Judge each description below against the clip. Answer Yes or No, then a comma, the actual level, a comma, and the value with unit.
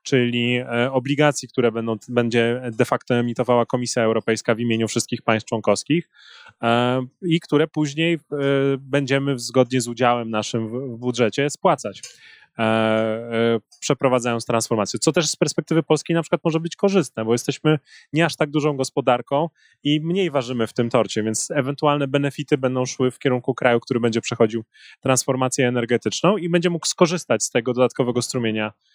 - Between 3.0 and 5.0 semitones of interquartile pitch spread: Yes, average, 3.9 semitones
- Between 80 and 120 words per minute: No, average, 150 wpm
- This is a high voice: No, low, 125 Hz